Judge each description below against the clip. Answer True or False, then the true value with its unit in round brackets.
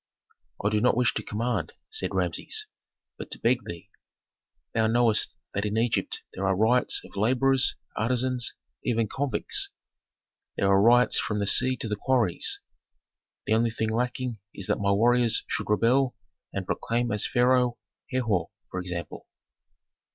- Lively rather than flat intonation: False (2.9 semitones)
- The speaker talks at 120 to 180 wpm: True (150 wpm)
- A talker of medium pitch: False (115 Hz)